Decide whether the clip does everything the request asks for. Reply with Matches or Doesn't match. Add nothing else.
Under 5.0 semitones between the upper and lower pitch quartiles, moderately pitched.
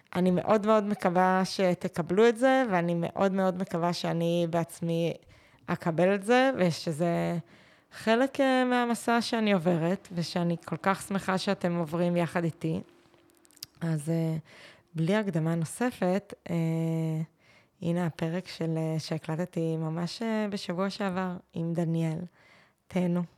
Matches